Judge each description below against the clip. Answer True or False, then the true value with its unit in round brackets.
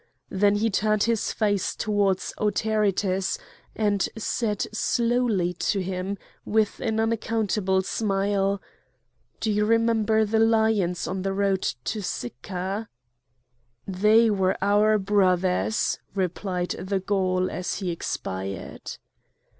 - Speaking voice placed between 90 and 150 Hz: False (200 Hz)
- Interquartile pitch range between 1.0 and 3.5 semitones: True (2.5 semitones)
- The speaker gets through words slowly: True (110 wpm)